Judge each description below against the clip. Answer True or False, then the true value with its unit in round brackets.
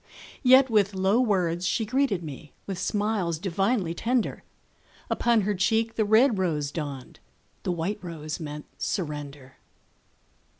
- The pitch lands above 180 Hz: True (190 Hz)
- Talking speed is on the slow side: True (130 wpm)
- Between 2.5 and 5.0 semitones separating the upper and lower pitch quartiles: False (5.5 semitones)